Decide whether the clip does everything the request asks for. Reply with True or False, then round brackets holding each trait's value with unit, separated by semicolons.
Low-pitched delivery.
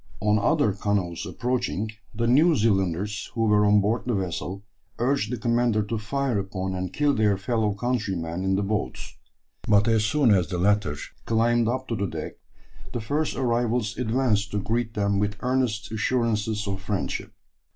True (105 Hz)